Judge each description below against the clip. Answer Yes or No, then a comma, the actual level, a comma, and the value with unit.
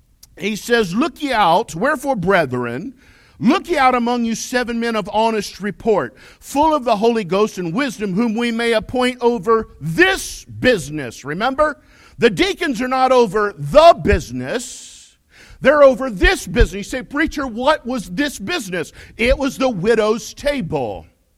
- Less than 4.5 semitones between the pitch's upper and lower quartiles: No, average, 4.8 semitones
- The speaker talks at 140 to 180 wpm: Yes, average, 155 wpm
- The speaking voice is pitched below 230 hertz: No, high, 235 Hz